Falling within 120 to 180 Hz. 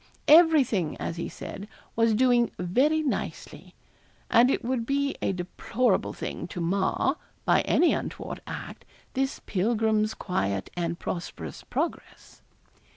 No: high, 220 Hz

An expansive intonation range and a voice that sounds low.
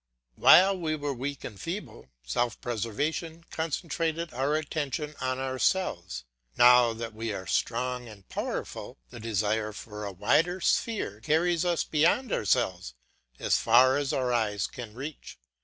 Yes: wide, 6.1 semitones; low, 130 Hz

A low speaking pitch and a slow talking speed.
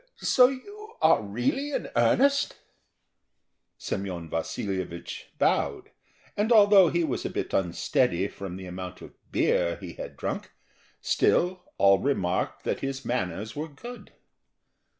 Yes: low, 120 Hz; slow, 130 wpm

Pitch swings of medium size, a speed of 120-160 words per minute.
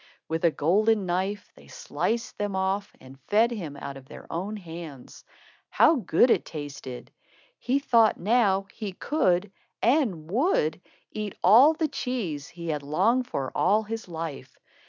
No: wide, 6.0 semitones; average, 155 wpm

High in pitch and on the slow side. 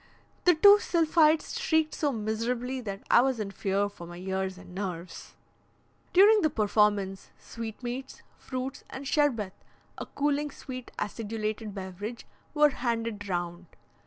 Yes: high, 230 Hz; slow, 130 wpm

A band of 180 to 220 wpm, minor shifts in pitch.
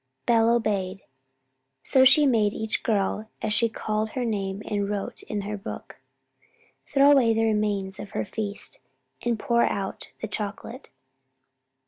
No: average, 150 wpm; narrow, 2.3 semitones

